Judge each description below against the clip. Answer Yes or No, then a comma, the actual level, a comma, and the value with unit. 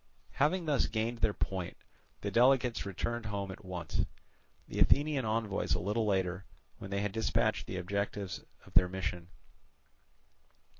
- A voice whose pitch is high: No, low, 105 Hz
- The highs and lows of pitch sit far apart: No, average, 3.7 semitones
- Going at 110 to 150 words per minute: Yes, average, 145 wpm